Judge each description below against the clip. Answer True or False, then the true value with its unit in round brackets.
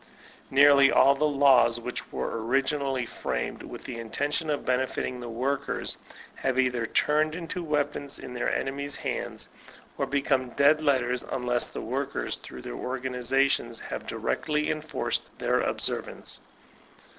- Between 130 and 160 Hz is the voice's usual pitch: True (135 Hz)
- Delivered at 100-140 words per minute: True (135 wpm)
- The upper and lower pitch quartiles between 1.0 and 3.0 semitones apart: True (2.5 semitones)